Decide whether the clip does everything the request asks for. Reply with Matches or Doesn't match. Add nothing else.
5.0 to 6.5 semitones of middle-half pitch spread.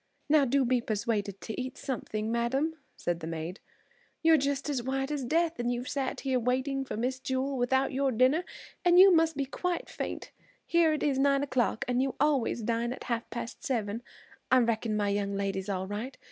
Doesn't match